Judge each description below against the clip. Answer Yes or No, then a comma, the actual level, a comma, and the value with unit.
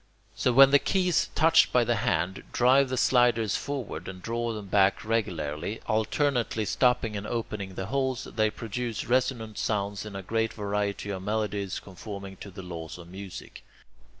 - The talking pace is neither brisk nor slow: Yes, average, 165 wpm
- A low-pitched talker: Yes, low, 110 Hz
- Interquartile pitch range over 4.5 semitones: No, average, 3.6 semitones